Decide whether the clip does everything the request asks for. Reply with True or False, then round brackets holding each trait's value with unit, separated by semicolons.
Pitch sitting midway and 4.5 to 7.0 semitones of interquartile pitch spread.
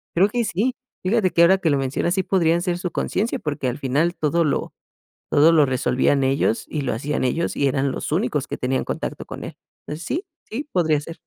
True (160 Hz; 4.8 semitones)